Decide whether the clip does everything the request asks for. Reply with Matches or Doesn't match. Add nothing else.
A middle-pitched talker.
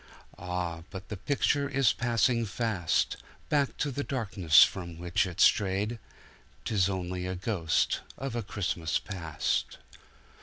Doesn't match